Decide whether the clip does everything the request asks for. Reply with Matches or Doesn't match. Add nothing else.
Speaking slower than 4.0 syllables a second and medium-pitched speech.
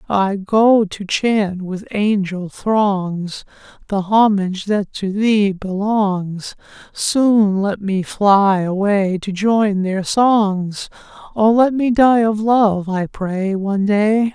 Doesn't match